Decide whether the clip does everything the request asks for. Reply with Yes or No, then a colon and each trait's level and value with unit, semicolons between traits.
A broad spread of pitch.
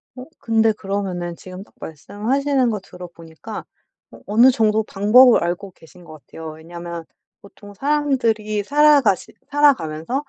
Yes: wide, 6.4 semitones